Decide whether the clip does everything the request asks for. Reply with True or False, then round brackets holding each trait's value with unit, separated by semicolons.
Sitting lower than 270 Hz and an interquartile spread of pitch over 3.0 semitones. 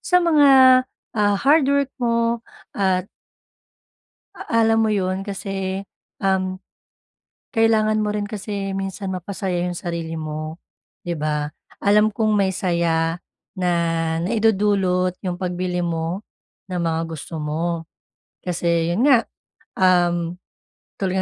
True (190 Hz; 3.7 semitones)